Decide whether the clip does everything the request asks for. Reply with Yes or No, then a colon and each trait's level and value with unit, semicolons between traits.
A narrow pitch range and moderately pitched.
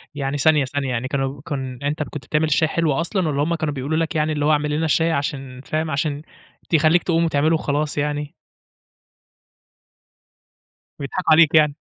Yes: narrow, 2.1 semitones; medium, 150 Hz